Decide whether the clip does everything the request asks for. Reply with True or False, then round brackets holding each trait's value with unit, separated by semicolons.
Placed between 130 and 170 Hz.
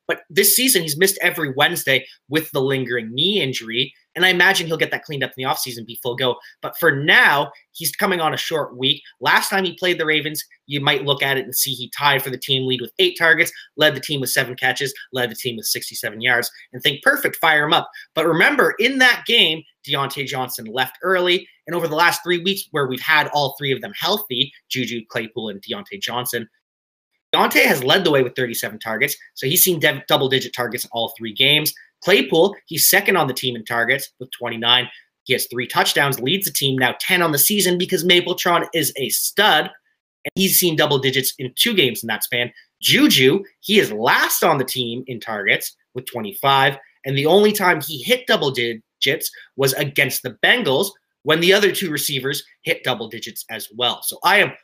True (140 Hz)